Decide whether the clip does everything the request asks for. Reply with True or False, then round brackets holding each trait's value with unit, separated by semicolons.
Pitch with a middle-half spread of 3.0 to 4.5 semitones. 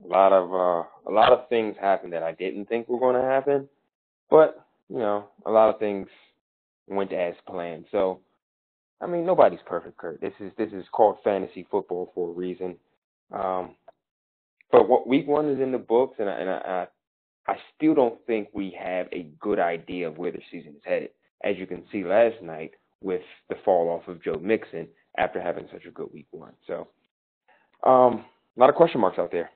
False (5.2 semitones)